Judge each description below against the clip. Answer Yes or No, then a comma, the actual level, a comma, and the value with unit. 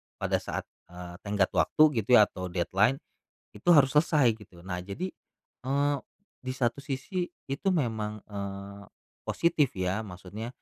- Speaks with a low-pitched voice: Yes, low, 110 Hz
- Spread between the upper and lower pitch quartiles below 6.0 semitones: No, wide, 6.3 semitones